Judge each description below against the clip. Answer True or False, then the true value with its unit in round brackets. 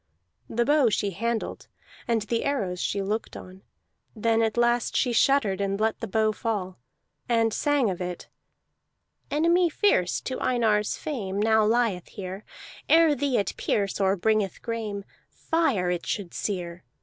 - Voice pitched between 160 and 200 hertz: False (220 Hz)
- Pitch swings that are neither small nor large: True (3.5 semitones)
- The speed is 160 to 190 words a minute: False (150 wpm)